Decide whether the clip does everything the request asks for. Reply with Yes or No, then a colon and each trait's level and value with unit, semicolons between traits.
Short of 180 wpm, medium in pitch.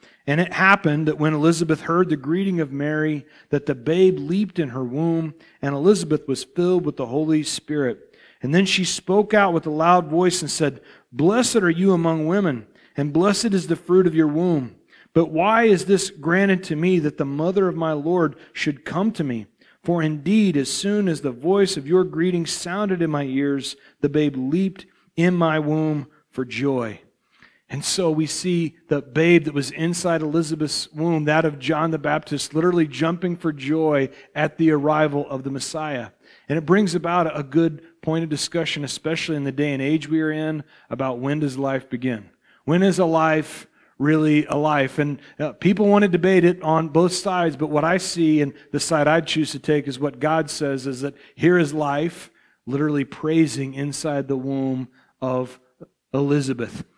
No: average, 190 wpm; medium, 155 Hz